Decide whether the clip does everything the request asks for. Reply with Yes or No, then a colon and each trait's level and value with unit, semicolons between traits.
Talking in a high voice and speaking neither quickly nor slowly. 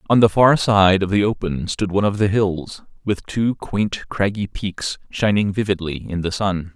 No: low, 100 Hz; average, 195 wpm